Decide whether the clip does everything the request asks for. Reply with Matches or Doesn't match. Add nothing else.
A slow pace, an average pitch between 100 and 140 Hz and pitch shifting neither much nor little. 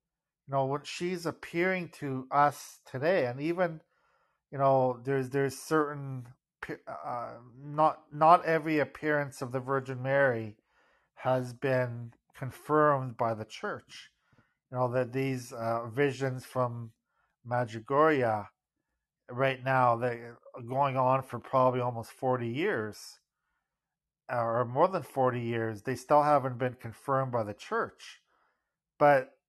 Matches